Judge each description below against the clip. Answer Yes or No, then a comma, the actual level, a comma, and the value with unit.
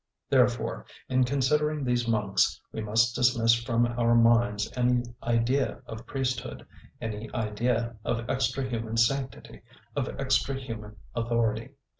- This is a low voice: Yes, low, 120 Hz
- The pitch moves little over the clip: Yes, narrow, 2.1 semitones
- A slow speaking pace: Yes, slow, 125 wpm